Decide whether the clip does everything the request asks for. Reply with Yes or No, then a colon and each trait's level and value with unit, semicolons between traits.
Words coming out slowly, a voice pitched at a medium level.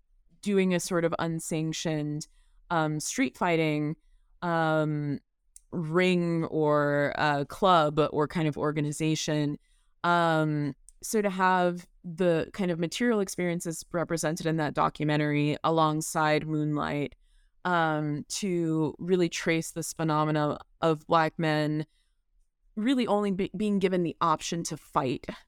Yes: slow, 120 wpm; medium, 160 Hz